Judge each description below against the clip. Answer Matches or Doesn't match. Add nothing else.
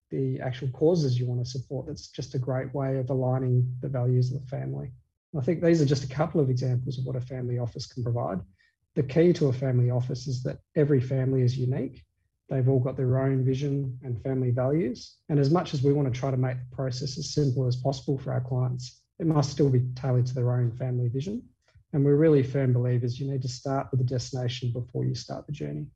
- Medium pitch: Doesn't match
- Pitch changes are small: Matches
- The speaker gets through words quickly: Matches